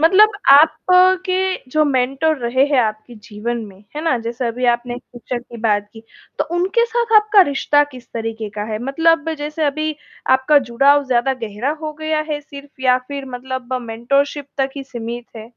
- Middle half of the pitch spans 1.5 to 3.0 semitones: No, average, 4.2 semitones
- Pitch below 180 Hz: No, very high, 265 Hz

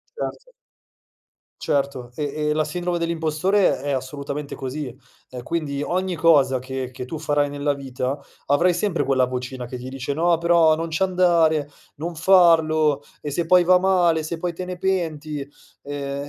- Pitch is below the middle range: No, medium, 155 Hz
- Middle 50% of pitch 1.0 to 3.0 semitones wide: No, average, 3.6 semitones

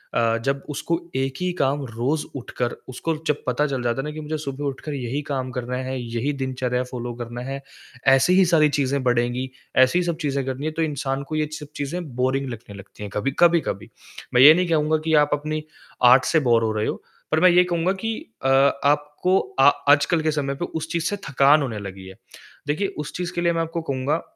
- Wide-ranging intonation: No, average, 3.6 semitones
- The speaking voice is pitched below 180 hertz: Yes, medium, 140 Hz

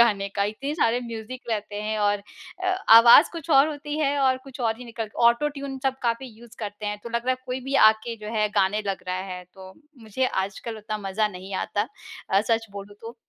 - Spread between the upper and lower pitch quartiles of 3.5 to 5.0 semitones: Yes, average, 3.8 semitones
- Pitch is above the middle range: Yes, high, 225 Hz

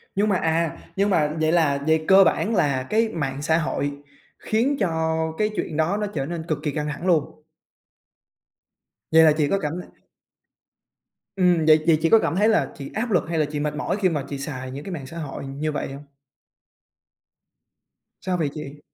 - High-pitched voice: No, medium, 160 Hz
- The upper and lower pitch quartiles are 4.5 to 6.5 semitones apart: No, average, 3.9 semitones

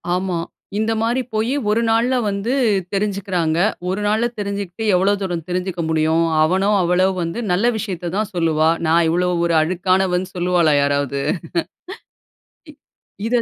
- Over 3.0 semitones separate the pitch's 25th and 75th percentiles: Yes, average, 3.5 semitones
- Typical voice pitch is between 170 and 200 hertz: Yes, medium, 185 Hz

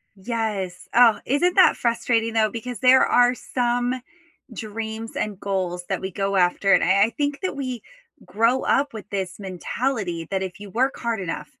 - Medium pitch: No, high, 225 Hz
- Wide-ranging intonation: No, average, 4.1 semitones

